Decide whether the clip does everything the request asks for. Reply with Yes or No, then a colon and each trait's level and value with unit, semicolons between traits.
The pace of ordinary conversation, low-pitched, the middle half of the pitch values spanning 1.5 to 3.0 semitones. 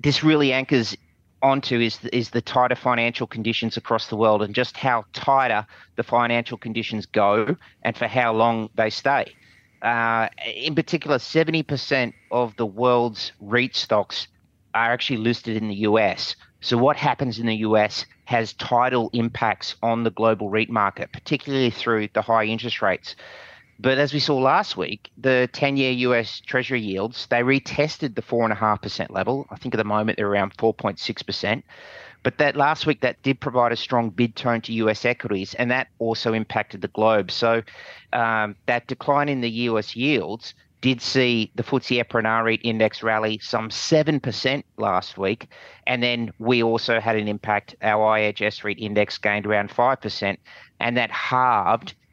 Yes: average, 180 wpm; low, 115 Hz; narrow, 2.6 semitones